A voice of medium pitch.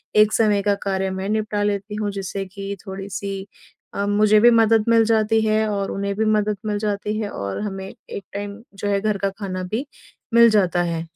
No: high, 205 Hz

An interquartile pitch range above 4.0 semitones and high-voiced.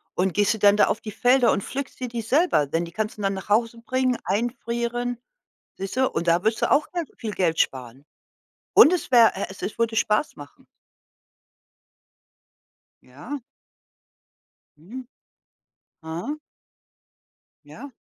Yes: average, 4.6 semitones; high, 220 Hz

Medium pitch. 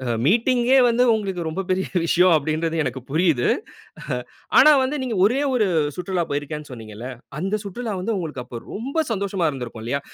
Yes: medium, 180 Hz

